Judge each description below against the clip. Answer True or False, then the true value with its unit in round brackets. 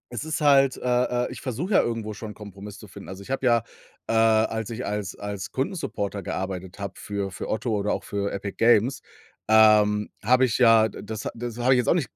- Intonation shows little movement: False (3.1 semitones)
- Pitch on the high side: False (110 Hz)